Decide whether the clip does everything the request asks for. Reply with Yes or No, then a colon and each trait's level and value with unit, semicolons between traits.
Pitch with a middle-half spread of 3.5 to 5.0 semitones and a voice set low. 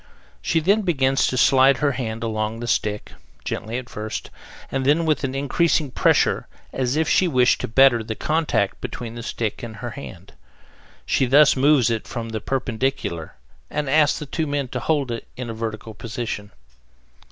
Yes: average, 4.0 semitones; low, 130 Hz